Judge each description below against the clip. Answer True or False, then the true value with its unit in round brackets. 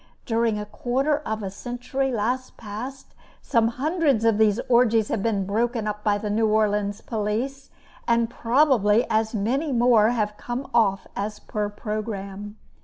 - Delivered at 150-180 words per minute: True (155 wpm)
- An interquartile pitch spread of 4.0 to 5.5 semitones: False (2.8 semitones)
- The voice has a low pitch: False (225 Hz)